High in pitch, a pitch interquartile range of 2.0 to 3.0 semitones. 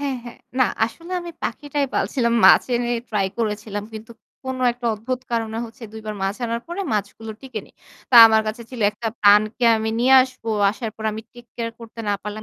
Yes: high, 230 Hz; narrow, 2.6 semitones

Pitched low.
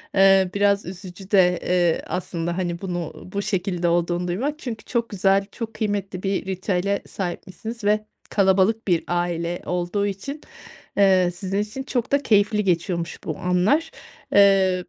No: high, 195 Hz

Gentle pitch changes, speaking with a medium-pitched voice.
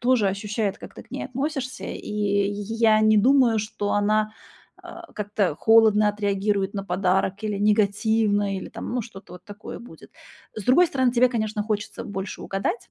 No: narrow, 2.0 semitones; high, 210 Hz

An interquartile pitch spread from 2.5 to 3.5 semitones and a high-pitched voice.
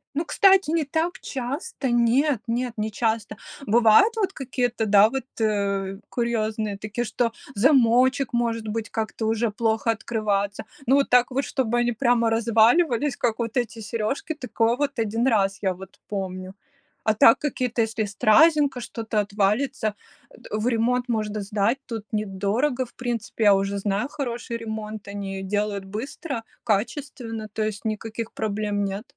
Yes: average, 2.9 semitones; high, 225 Hz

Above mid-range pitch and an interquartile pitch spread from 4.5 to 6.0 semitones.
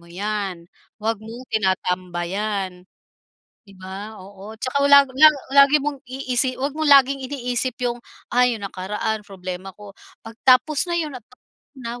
Yes: high, 225 Hz; average, 5.2 semitones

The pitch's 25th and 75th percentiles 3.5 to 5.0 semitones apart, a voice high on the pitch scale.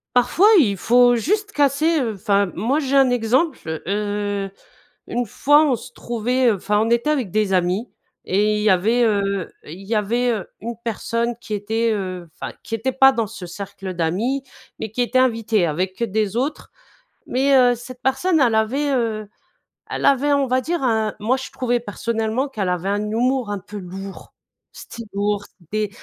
Yes: average, 4.0 semitones; high, 225 Hz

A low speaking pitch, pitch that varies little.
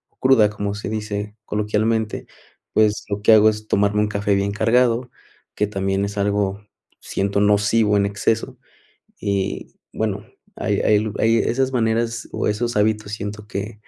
Yes: low, 105 Hz; narrow, 1.5 semitones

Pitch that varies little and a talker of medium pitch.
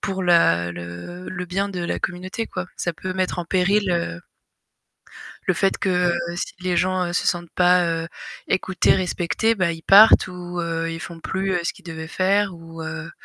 Yes: narrow, 1.9 semitones; medium, 175 Hz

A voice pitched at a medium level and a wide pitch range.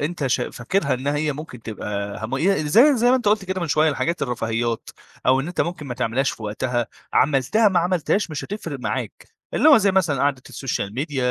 Yes: medium, 145 Hz; wide, 6.5 semitones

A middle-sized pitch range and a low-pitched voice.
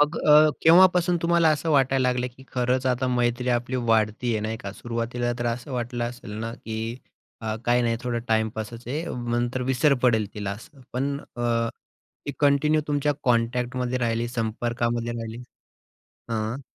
No: narrow, 2.3 semitones; low, 120 Hz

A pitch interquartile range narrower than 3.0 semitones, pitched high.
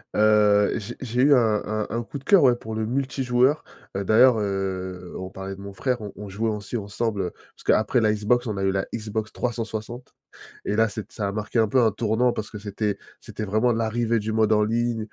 No: narrow, 2.5 semitones; low, 110 Hz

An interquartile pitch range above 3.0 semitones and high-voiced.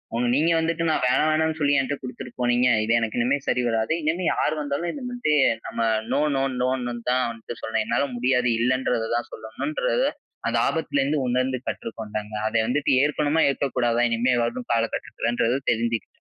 No: average, 4.0 semitones; low, 125 Hz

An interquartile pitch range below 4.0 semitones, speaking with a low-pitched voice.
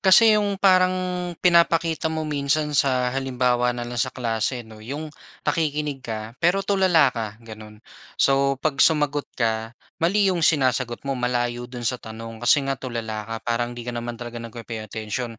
No: average, 4.6 semitones; low, 125 Hz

